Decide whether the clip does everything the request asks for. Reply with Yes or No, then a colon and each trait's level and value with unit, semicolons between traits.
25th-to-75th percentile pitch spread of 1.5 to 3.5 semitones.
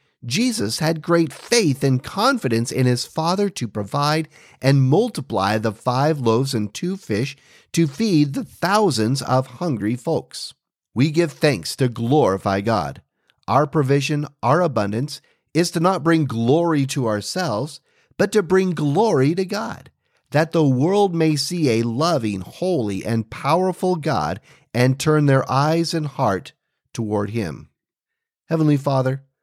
No: wide, 5.6 semitones